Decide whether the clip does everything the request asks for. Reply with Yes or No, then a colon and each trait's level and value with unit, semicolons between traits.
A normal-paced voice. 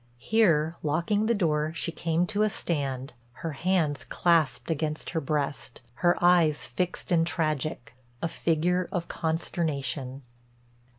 No: slow, 130 wpm